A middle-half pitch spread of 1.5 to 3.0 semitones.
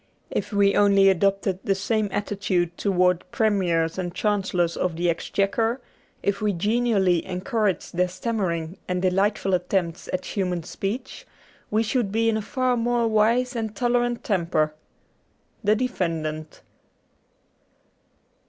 No: average, 3.5 semitones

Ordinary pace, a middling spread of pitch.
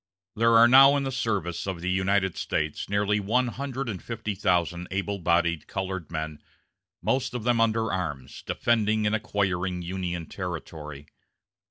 Yes: average, 155 wpm; average, 4.5 semitones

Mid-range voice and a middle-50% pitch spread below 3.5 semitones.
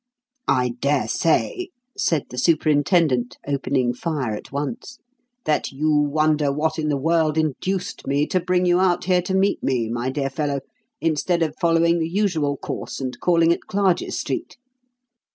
No: medium, 155 Hz; average, 3.8 semitones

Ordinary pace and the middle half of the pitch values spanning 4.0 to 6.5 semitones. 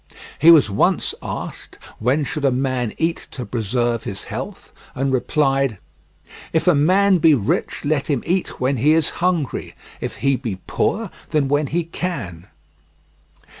Yes: average, 155 wpm; average, 4.6 semitones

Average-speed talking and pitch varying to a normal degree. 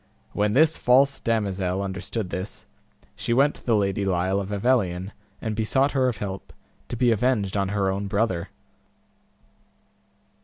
Yes: average, 150 wpm; average, 3.8 semitones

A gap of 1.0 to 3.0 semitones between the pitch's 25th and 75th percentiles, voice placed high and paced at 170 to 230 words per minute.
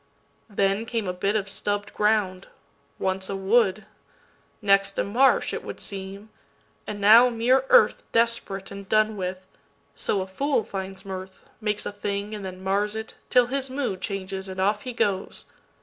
No: narrow, 2.4 semitones; high, 200 Hz; average, 150 wpm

